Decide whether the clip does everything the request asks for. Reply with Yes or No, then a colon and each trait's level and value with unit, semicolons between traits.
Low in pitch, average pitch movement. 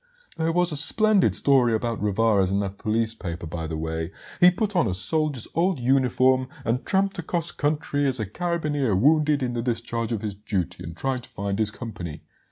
No: low, 120 Hz; wide, 6.8 semitones